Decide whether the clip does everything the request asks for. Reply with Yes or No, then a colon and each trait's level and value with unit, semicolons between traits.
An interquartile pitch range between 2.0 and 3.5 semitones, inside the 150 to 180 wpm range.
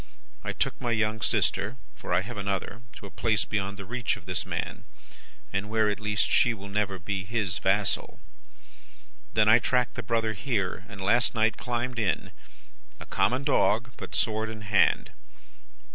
Yes: average, 2.7 semitones; average, 175 wpm